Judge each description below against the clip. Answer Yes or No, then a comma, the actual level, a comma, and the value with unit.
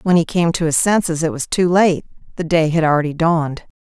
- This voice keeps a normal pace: No, fast, 235 wpm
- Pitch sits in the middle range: Yes, medium, 165 Hz